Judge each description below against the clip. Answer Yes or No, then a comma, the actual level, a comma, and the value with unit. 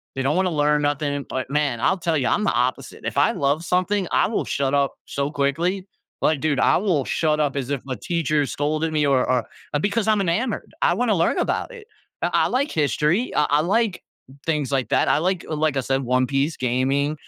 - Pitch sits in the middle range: Yes, medium, 150 Hz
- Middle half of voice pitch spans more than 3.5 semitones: Yes, average, 4.2 semitones